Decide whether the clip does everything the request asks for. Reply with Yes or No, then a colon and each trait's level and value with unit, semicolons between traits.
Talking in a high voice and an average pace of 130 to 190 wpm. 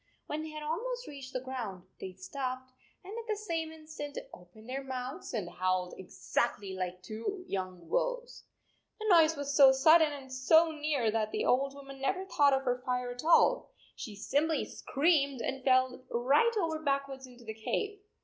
Yes: very high, 270 Hz; average, 180 wpm